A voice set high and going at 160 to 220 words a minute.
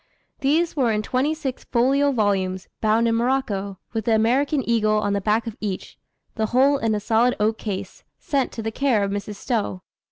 Yes: high, 225 Hz; average, 195 wpm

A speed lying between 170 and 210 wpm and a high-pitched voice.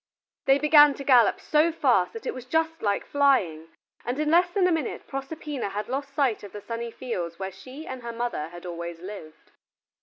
Yes: fast, 205 wpm; very high, 255 Hz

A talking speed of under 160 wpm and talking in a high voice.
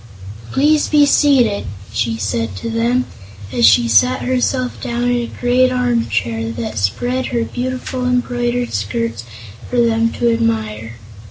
Yes: average, 145 wpm; high, 235 Hz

